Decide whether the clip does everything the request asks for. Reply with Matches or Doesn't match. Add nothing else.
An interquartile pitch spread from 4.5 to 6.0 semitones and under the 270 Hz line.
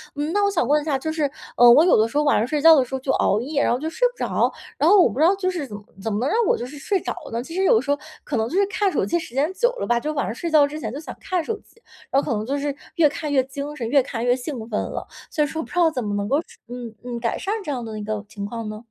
Doesn't match